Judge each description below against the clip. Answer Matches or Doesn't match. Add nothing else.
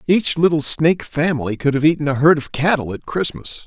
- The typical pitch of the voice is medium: Matches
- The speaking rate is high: Matches